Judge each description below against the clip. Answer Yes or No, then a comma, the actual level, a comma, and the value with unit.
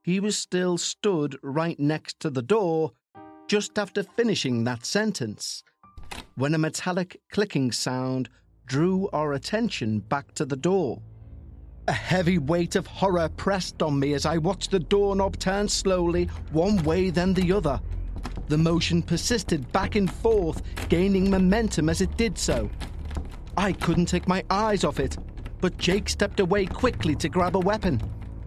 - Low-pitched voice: No, medium, 170 Hz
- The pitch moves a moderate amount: No, wide, 6.9 semitones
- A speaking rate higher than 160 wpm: No, average, 155 wpm